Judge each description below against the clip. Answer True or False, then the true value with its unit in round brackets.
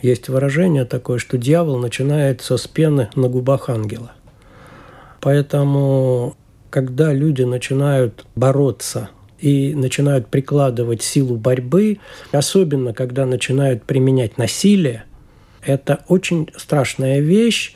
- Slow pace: True (100 wpm)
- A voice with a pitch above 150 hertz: False (135 Hz)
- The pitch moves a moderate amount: False (2.3 semitones)